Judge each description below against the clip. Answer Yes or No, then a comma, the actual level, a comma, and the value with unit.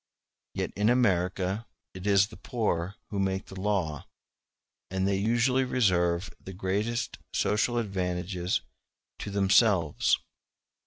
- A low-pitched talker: Yes, low, 100 Hz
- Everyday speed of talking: No, slow, 115 wpm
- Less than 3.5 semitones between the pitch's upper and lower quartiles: Yes, average, 3.0 semitones